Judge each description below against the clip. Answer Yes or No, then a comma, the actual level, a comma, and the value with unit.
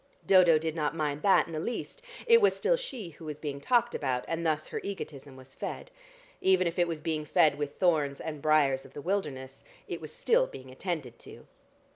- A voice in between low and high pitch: Yes, medium, 155 Hz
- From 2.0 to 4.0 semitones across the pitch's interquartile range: No, average, 4.7 semitones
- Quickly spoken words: Yes, fast, 210 wpm